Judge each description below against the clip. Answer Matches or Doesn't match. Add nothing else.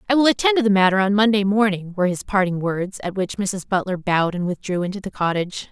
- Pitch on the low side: Doesn't match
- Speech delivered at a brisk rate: Matches